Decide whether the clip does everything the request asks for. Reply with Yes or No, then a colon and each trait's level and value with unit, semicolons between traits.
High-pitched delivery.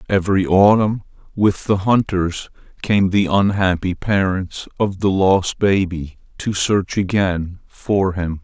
No: very low, 95 Hz